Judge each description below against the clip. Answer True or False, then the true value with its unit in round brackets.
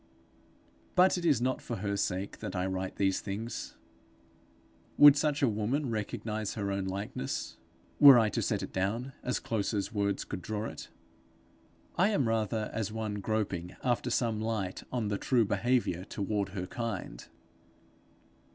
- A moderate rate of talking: True (160 wpm)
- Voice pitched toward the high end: False (110 Hz)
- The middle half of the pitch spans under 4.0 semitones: True (3.4 semitones)